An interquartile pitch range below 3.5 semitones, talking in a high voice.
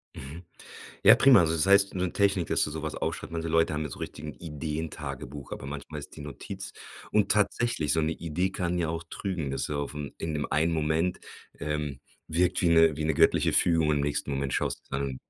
No: average, 2.7 semitones; very low, 80 Hz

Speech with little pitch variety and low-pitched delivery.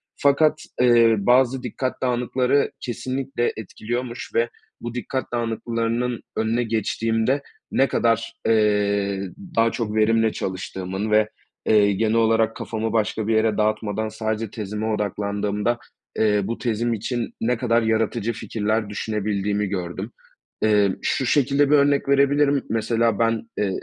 Yes: narrow, 2.3 semitones; low, 115 Hz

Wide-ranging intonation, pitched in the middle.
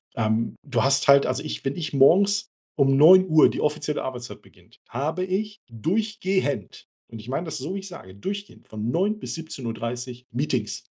Yes: wide, 7.1 semitones; medium, 145 Hz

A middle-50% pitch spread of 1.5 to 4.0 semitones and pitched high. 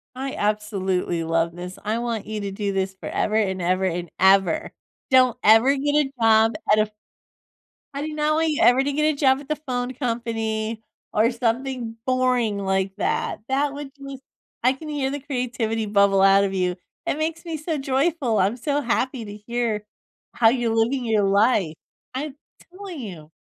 No: average, 5.1 semitones; high, 230 Hz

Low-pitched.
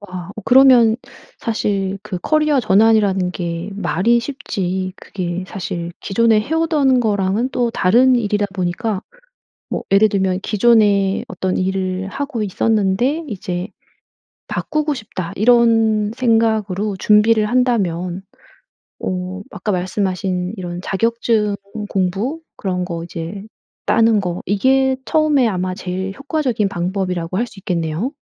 No: high, 205 Hz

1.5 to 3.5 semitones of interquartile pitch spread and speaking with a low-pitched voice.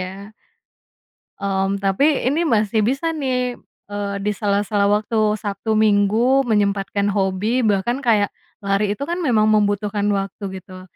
No: average, 2.9 semitones; high, 210 Hz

